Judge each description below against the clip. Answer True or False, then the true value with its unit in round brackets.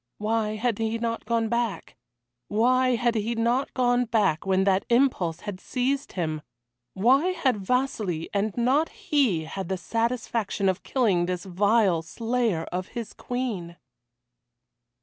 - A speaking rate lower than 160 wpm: True (140 wpm)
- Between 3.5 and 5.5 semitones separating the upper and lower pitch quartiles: True (4.5 semitones)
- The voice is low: False (225 Hz)